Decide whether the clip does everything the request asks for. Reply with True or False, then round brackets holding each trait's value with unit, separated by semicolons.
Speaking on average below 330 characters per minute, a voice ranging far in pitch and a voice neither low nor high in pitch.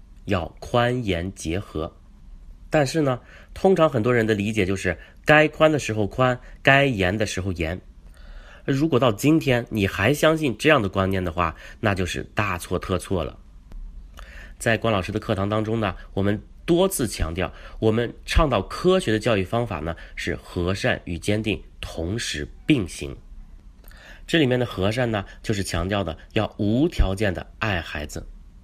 False (235 characters per minute; 6.0 semitones; 95 Hz)